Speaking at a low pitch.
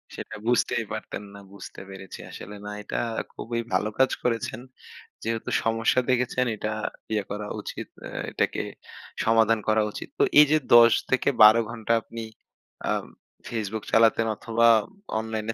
Yes: low, 115 Hz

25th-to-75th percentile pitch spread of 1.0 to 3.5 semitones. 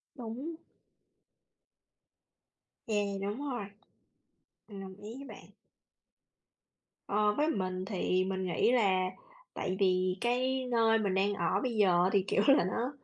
No: average, 4.2 semitones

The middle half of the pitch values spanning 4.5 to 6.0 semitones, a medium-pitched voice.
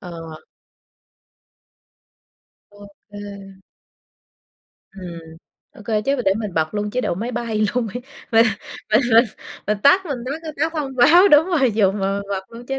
No: average, 5.3 semitones; high, 220 Hz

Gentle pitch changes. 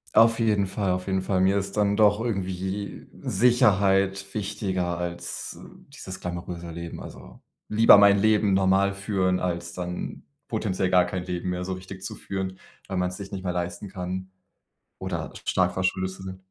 Yes: narrow, 1.7 semitones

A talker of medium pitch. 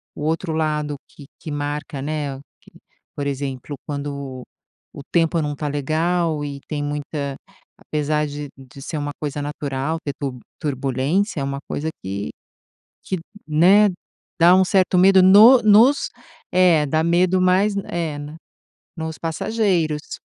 Yes: medium, 150 Hz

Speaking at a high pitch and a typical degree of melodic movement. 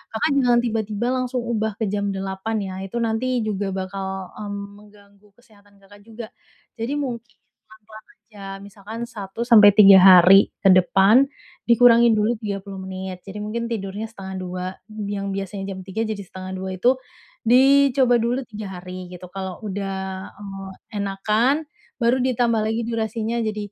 Yes: high, 210 Hz; average, 3.1 semitones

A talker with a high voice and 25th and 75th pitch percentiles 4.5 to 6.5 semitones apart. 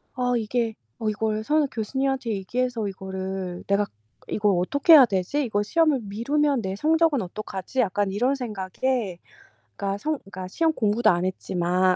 Yes: high, 215 Hz; wide, 5.5 semitones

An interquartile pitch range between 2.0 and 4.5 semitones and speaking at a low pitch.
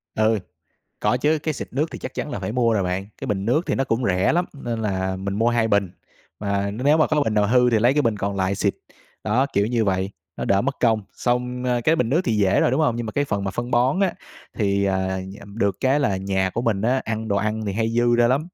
Yes: average, 4.1 semitones; low, 110 Hz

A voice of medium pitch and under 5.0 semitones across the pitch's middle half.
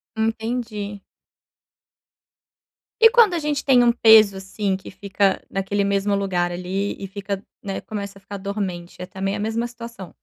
No: high, 200 Hz; narrow, 2.5 semitones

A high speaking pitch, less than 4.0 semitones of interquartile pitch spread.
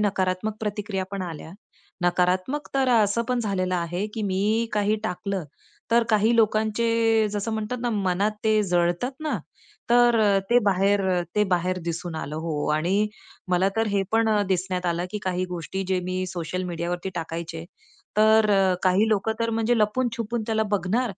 Yes: high, 200 Hz; average, 3.4 semitones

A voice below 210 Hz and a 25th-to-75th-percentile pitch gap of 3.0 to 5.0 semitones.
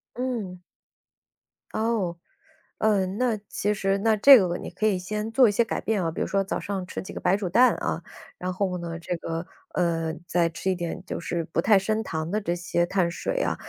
Yes: high, 190 Hz; average, 3.8 semitones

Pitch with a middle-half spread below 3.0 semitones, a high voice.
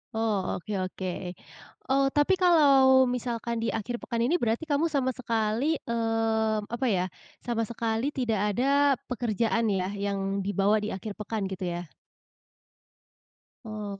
No: average, 3.7 semitones; high, 225 Hz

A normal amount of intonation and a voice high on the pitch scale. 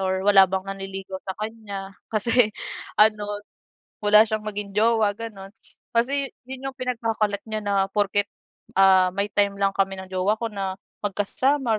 No: narrow, 2.3 semitones; high, 205 Hz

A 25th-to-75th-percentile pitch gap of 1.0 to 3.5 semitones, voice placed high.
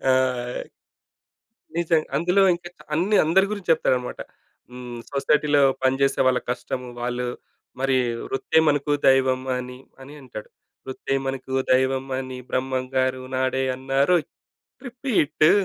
No: average, 3.1 semitones; low, 135 Hz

